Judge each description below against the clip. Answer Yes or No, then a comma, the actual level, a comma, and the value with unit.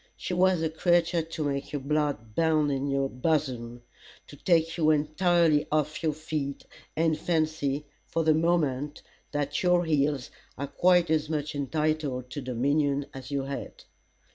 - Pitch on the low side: No, medium, 150 Hz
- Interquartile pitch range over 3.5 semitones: No, narrow, 2.5 semitones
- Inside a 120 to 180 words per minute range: Yes, average, 155 wpm